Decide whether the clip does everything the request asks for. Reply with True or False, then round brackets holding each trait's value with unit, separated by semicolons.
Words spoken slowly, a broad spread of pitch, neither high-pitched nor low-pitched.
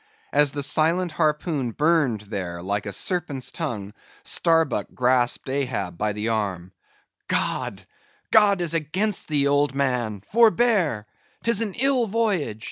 True (125 wpm; 8.4 semitones; 145 Hz)